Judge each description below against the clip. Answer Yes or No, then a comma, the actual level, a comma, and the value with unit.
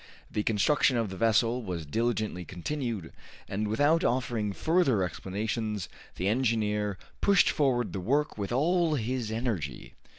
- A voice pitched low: Yes, low, 110 Hz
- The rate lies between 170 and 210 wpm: No, slow, 135 wpm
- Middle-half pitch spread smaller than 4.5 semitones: Yes, average, 4.1 semitones